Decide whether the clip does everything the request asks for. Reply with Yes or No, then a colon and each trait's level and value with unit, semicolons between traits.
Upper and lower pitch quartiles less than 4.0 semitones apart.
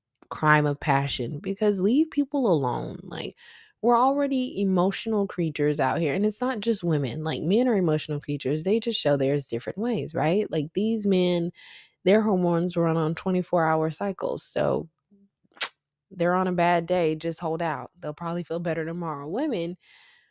No: average, 4.7 semitones